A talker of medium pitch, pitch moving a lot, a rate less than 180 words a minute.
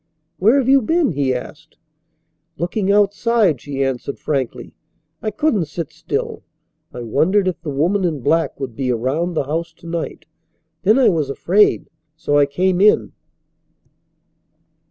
Yes: medium, 170 Hz; wide, 6.5 semitones; average, 150 wpm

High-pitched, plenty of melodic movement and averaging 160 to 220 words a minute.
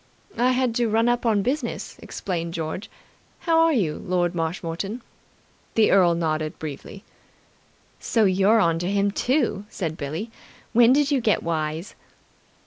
No: high, 195 Hz; wide, 6.0 semitones; average, 145 wpm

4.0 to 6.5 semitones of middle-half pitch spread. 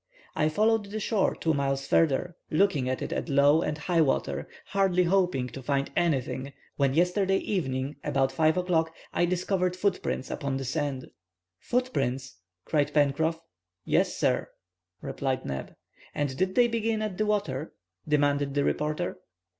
Yes: average, 5.0 semitones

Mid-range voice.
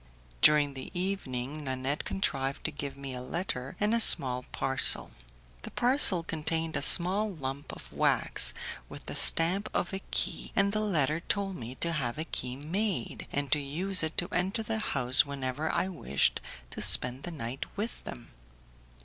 Yes: medium, 150 Hz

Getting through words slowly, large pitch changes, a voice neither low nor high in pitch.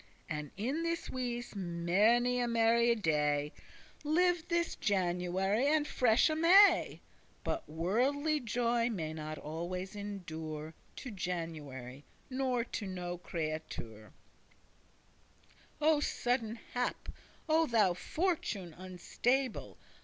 No: slow, 100 wpm; wide, 7.2 semitones; high, 210 Hz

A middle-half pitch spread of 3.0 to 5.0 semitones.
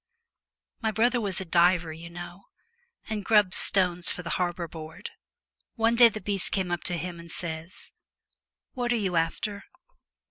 Yes: average, 3.7 semitones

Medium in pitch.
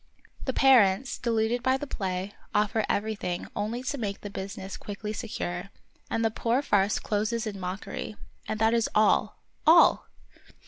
No: high, 215 Hz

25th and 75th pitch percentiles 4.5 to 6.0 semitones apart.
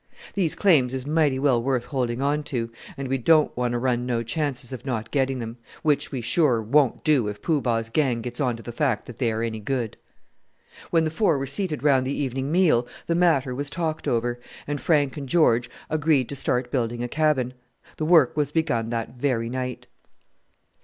No: average, 3.8 semitones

